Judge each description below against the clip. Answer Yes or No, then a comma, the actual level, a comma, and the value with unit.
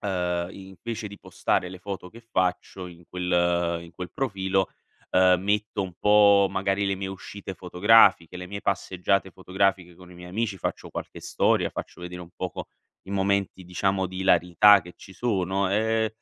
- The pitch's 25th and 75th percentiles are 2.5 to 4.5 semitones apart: No, narrow, 1.9 semitones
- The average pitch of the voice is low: Yes, very low, 95 Hz